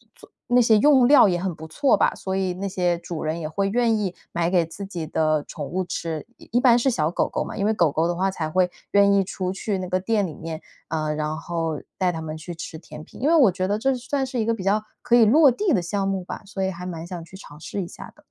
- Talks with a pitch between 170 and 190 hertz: Yes, medium, 185 Hz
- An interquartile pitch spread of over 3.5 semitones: Yes, average, 4.2 semitones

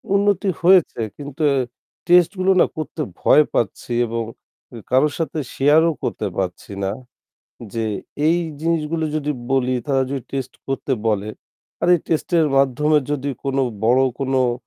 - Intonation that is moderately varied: Yes, average, 4.2 semitones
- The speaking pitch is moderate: Yes, medium, 145 Hz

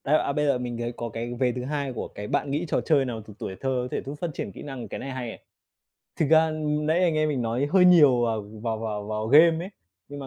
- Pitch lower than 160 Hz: Yes, low, 135 Hz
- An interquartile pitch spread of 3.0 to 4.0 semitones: No, average, 4.4 semitones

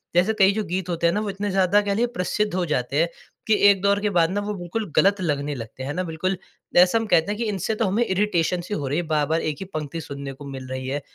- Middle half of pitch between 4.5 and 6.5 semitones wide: Yes, average, 5.0 semitones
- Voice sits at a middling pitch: Yes, medium, 180 Hz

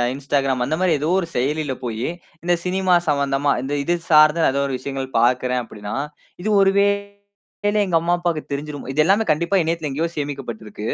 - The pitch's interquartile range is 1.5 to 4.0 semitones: No, average, 4.5 semitones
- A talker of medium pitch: Yes, medium, 150 Hz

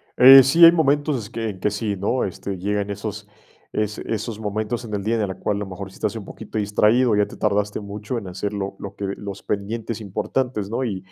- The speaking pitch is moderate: No, low, 105 Hz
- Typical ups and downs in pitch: No, narrow, 2.3 semitones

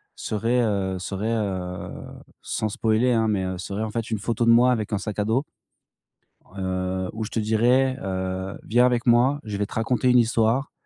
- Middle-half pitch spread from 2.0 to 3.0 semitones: No, average, 3.4 semitones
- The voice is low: Yes, low, 110 Hz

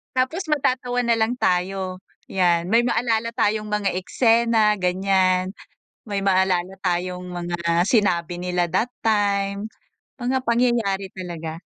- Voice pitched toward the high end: Yes, high, 195 Hz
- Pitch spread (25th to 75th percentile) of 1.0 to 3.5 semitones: No, average, 4.0 semitones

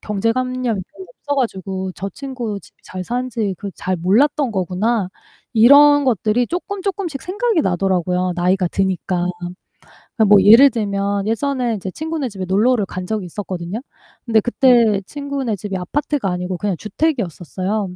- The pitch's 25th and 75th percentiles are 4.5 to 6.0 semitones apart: Yes, wide, 5.4 semitones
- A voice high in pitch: Yes, high, 215 Hz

